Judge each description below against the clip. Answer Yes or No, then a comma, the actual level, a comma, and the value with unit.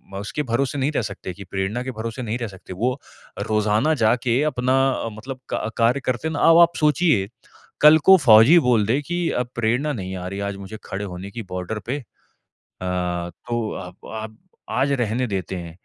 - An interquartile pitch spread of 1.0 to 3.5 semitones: No, average, 5.0 semitones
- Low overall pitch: Yes, low, 115 Hz